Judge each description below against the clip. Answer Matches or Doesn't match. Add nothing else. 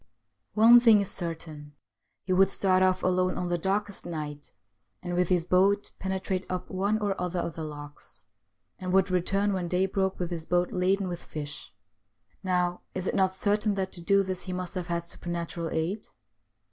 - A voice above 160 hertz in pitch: Matches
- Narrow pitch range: Matches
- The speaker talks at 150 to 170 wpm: Doesn't match